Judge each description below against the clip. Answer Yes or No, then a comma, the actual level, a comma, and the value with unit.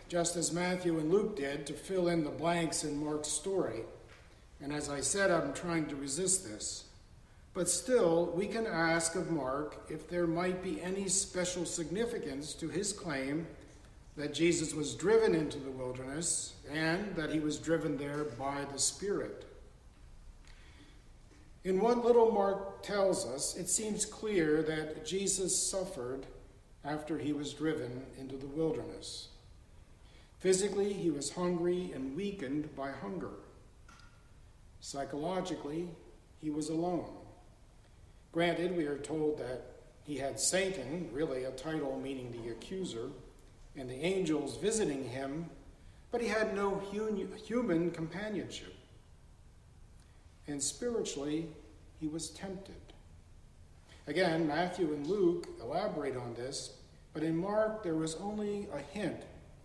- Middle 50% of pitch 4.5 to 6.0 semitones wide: Yes, average, 5.3 semitones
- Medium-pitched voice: Yes, medium, 155 Hz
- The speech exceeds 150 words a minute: No, slow, 135 wpm